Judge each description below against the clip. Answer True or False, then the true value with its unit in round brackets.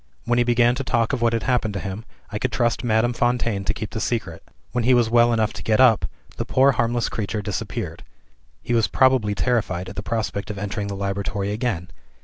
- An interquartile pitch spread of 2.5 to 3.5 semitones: True (2.8 semitones)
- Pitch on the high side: False (115 Hz)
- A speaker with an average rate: False (220 wpm)